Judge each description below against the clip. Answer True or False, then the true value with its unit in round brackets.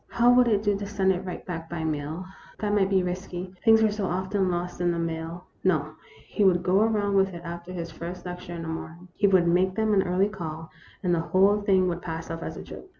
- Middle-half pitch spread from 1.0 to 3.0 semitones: True (2.6 semitones)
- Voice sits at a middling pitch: True (180 Hz)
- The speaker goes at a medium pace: False (255 wpm)